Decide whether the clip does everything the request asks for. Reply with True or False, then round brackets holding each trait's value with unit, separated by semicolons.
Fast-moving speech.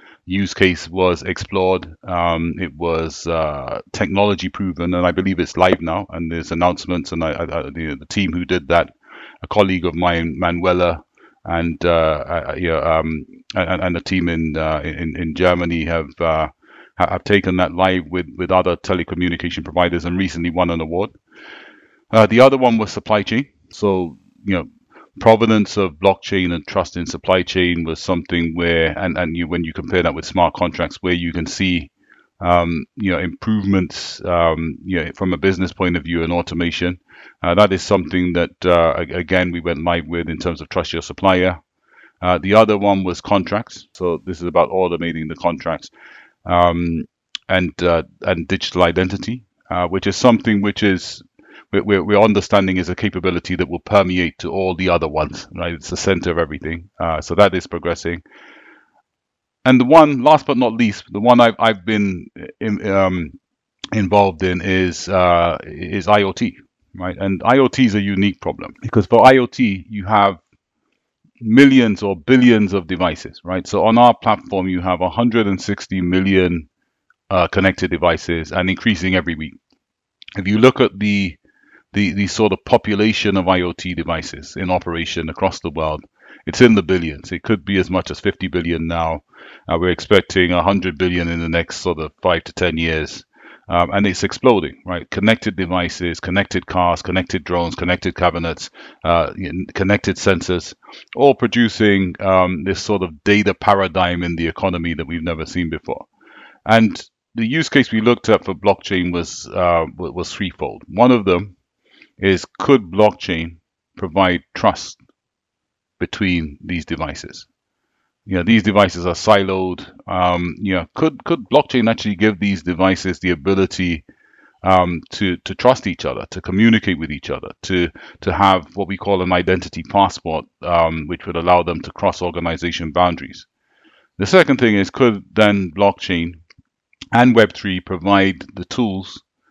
False (170 wpm)